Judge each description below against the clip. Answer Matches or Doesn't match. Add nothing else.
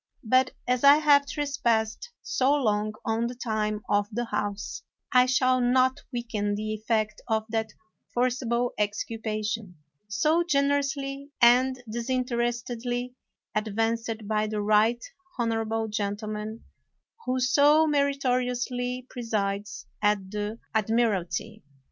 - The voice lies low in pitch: Doesn't match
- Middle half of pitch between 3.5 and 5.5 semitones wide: Doesn't match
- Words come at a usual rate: Doesn't match